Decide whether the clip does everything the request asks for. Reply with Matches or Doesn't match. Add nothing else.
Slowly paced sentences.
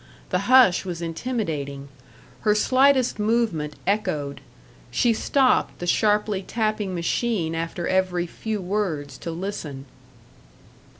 Matches